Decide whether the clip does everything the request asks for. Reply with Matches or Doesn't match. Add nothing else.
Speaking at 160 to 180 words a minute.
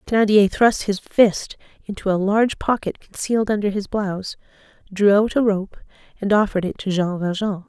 Matches